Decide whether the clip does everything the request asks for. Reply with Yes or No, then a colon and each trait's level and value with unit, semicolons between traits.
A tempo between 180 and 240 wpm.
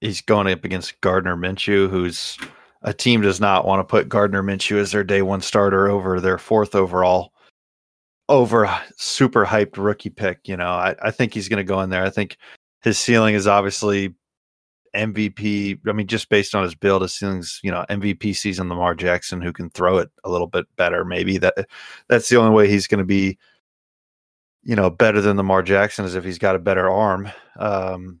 Yes: average, 200 wpm